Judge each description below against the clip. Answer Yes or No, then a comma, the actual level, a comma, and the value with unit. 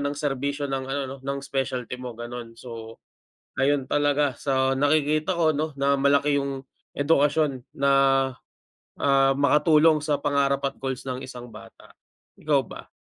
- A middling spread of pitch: No, narrow, 1.7 semitones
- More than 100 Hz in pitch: Yes, medium, 140 Hz